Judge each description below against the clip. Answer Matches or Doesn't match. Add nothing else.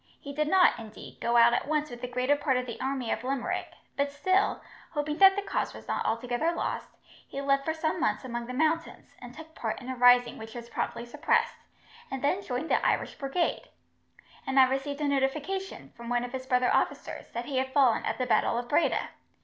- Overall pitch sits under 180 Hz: Doesn't match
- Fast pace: Matches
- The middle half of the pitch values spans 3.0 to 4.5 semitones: Matches